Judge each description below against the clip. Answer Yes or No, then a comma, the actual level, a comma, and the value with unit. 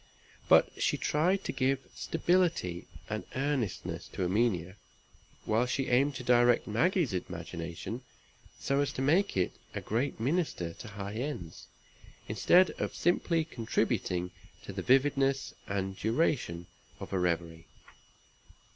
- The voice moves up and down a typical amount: No, wide, 7.4 semitones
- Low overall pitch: Yes, low, 120 Hz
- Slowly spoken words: Yes, slow, 130 wpm